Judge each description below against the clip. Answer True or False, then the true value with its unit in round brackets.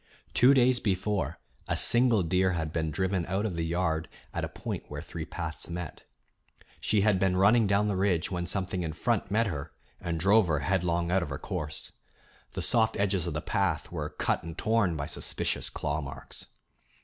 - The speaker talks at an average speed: True (195 wpm)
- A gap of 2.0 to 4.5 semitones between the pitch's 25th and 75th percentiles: True (3.6 semitones)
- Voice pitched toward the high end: False (90 Hz)